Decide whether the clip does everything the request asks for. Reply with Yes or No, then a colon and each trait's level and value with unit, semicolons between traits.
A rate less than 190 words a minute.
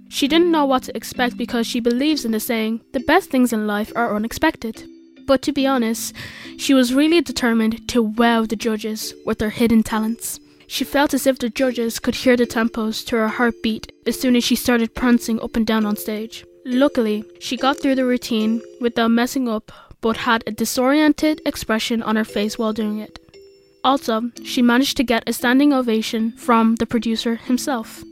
No: average, 195 wpm